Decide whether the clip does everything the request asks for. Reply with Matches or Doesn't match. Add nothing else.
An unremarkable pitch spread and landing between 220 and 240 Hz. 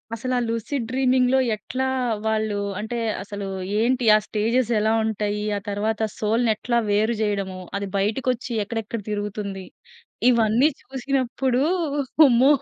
Matches